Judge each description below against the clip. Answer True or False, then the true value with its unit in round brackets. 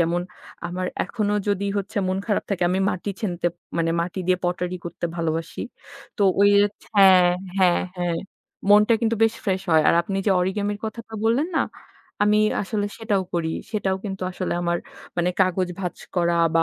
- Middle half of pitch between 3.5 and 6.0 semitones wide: False (2.8 semitones)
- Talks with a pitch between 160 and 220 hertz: True (190 Hz)